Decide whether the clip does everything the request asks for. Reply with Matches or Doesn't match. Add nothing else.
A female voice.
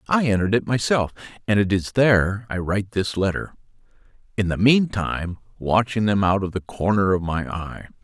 Doesn't match